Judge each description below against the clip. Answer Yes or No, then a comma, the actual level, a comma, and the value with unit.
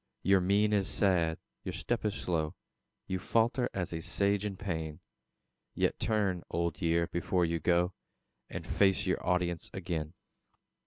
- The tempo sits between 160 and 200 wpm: No, average, 150 wpm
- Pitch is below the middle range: Yes, very low, 90 Hz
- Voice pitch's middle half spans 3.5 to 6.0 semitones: No, average, 2.8 semitones